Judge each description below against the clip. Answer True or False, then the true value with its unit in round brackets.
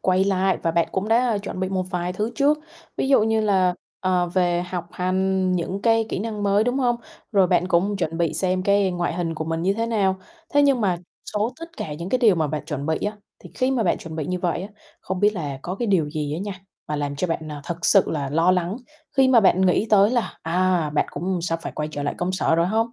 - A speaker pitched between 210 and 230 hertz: False (185 Hz)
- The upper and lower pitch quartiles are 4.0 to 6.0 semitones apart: False (3.6 semitones)